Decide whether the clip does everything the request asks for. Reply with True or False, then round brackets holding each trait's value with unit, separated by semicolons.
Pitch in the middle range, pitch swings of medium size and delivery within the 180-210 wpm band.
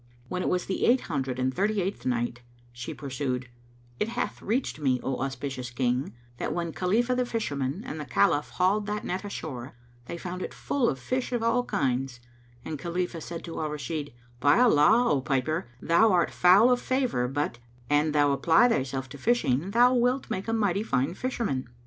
False (165 Hz; 8.1 semitones; 190 wpm)